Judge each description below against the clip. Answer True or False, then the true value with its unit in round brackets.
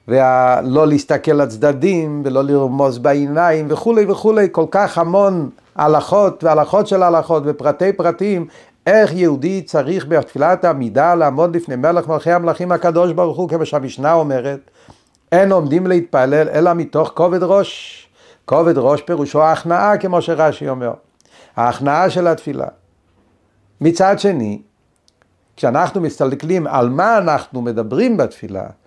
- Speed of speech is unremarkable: True (130 wpm)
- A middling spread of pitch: True (3.9 semitones)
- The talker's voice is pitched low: False (160 Hz)